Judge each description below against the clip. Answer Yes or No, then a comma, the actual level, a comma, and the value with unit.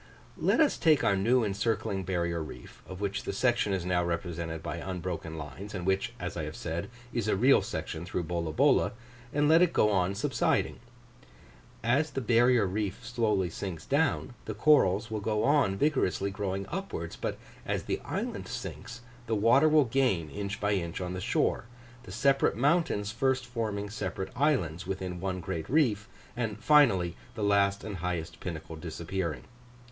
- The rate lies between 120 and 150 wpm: No, average, 170 wpm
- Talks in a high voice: No, low, 100 Hz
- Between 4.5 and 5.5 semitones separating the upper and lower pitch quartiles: Yes, average, 5.1 semitones